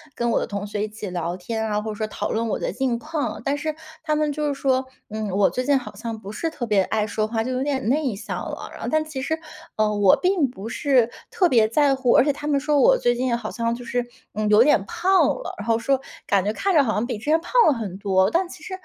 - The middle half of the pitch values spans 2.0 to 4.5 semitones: No, average, 5.3 semitones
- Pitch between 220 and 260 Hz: Yes, high, 240 Hz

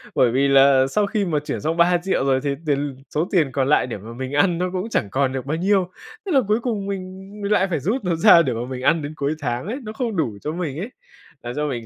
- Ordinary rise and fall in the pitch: No, wide, 6.1 semitones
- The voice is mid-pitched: Yes, medium, 160 Hz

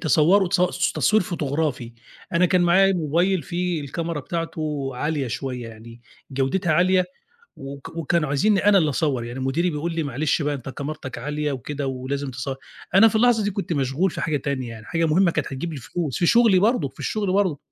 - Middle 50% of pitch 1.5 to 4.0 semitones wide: No, average, 4.8 semitones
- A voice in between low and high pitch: Yes, medium, 155 Hz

